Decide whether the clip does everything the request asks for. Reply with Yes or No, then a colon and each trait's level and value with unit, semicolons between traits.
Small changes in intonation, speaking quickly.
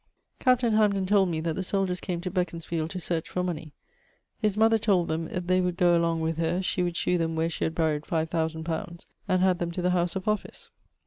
Yes: narrow, 2.3 semitones; fast, 240 wpm